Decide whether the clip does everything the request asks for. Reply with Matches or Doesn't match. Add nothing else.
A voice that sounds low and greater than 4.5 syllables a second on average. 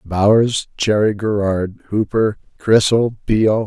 Doesn't match